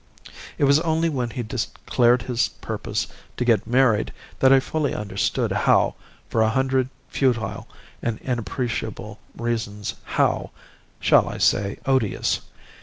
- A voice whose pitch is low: Yes, low, 120 Hz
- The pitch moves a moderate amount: Yes, average, 3.3 semitones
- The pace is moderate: No, slow, 130 wpm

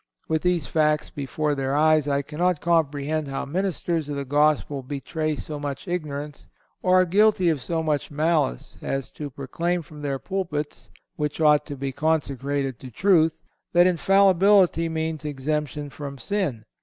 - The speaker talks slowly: No, average, 155 wpm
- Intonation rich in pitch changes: No, average, 3.0 semitones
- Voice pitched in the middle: Yes, medium, 150 Hz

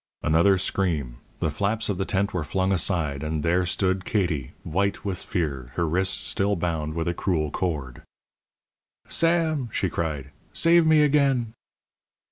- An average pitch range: Yes, average, 4.4 semitones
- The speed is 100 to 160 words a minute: Yes, average, 150 wpm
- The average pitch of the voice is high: No, very low, 90 Hz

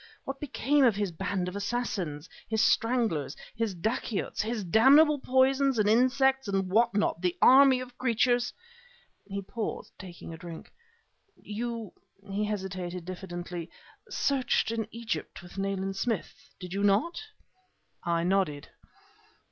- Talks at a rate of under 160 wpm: Yes, average, 140 wpm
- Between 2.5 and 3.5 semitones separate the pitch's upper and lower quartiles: No, average, 4.8 semitones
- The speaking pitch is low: No, high, 210 Hz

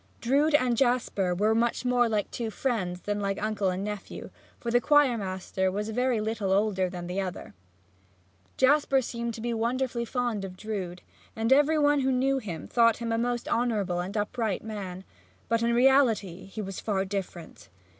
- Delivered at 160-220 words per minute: Yes, average, 180 wpm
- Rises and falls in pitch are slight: No, average, 4.0 semitones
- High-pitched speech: Yes, high, 220 Hz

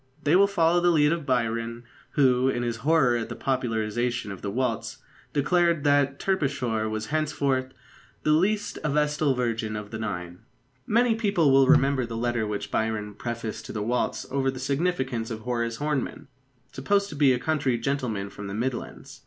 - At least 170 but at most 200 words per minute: Yes, average, 180 wpm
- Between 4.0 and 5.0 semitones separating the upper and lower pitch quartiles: Yes, average, 4.6 semitones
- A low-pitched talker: Yes, low, 130 Hz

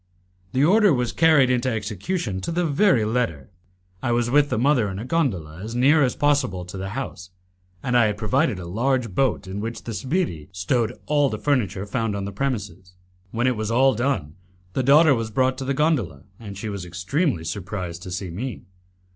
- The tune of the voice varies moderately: No, wide, 5.8 semitones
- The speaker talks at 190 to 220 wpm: Yes, average, 200 wpm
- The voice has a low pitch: Yes, low, 115 Hz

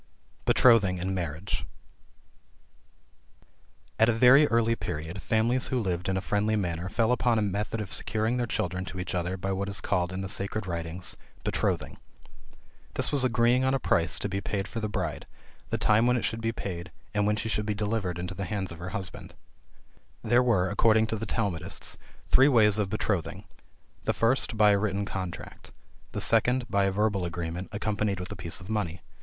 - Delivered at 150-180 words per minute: No, average, 195 wpm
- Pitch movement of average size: Yes, average, 3.5 semitones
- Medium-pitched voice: No, low, 100 Hz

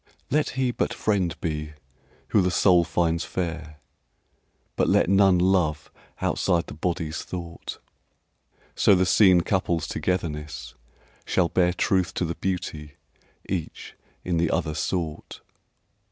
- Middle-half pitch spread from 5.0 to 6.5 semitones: No, average, 2.8 semitones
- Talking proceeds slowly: Yes, slow, 125 wpm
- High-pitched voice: No, very low, 85 Hz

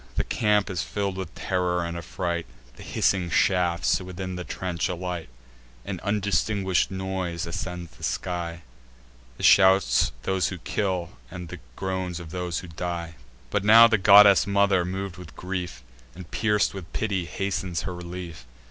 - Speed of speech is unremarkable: Yes, average, 155 wpm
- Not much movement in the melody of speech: Yes, narrow, 1.9 semitones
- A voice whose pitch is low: Yes, very low, 90 Hz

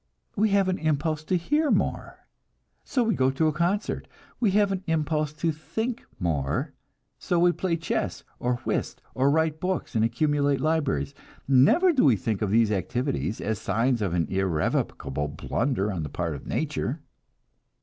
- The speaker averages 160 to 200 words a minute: Yes, average, 170 wpm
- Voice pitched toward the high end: No, medium, 145 Hz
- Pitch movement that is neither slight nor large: No, wide, 8.3 semitones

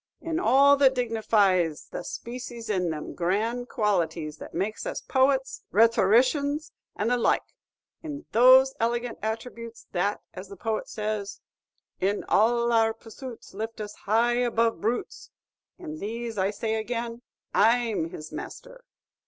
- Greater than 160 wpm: No, average, 140 wpm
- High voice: Yes, high, 230 Hz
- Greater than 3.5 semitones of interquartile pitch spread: No, average, 3.0 semitones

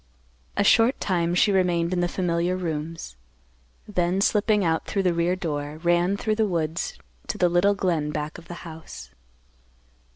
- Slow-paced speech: No, average, 165 wpm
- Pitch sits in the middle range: Yes, medium, 175 Hz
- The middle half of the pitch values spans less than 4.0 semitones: Yes, narrow, 2.5 semitones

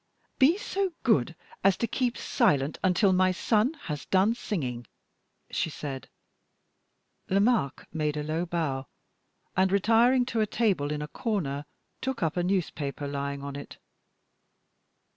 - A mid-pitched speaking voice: Yes, medium, 180 Hz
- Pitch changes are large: Yes, wide, 7.6 semitones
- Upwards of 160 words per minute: No, average, 140 wpm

